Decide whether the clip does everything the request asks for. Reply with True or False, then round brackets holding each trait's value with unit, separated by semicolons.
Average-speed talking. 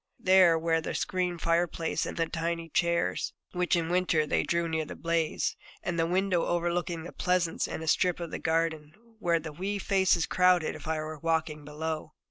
True (195 wpm)